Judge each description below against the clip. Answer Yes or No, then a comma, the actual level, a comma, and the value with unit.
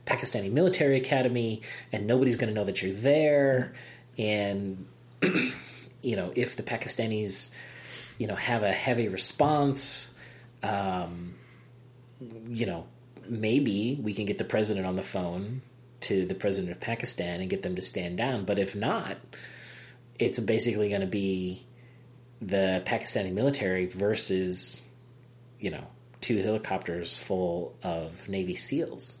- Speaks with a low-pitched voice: Yes, low, 110 Hz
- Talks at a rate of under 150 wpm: Yes, slow, 135 wpm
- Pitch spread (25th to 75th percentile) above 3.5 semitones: Yes, average, 4.5 semitones